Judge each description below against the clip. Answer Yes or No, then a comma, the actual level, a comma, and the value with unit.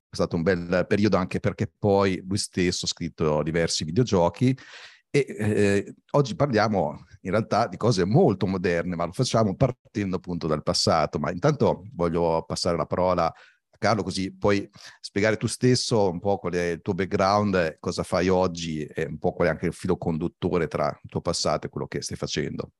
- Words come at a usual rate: No, fast, 190 wpm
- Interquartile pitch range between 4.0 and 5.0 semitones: No, average, 3.2 semitones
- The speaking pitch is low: Yes, very low, 95 Hz